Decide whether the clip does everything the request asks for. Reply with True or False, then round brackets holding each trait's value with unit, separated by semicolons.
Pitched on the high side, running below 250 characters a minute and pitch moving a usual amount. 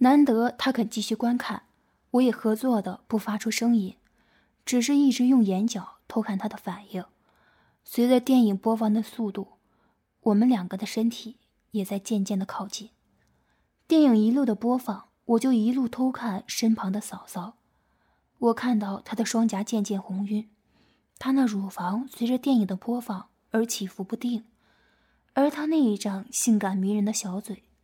True (225 Hz; 240 characters per minute; 3.1 semitones)